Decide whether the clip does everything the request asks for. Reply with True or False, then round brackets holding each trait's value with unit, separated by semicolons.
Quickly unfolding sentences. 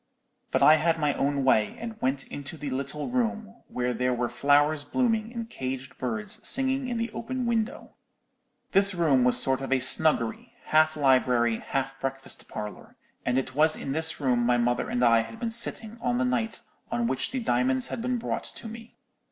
False (195 wpm)